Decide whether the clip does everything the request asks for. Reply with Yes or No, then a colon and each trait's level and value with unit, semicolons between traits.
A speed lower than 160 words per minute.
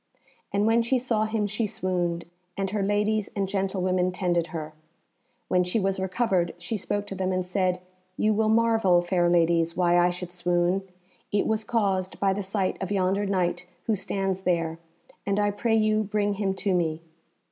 No: average, 180 wpm